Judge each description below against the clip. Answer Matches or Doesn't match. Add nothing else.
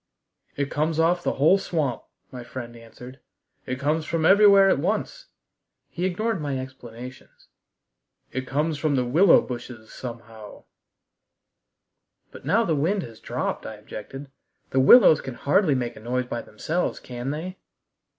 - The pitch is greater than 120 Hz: Matches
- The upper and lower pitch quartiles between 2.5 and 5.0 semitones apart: Doesn't match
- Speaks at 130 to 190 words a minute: Matches